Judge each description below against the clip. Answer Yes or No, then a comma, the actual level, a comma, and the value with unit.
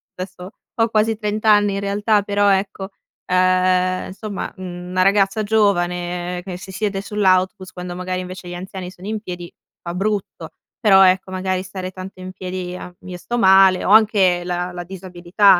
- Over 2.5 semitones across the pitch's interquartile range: No, narrow, 1.8 semitones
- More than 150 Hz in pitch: Yes, medium, 185 Hz